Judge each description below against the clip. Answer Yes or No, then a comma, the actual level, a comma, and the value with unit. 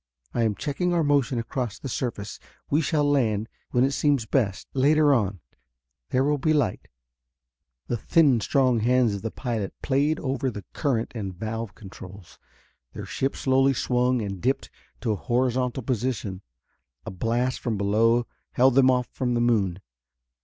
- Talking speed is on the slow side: No, average, 160 wpm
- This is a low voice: Yes, low, 125 Hz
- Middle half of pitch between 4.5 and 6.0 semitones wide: No, average, 3.7 semitones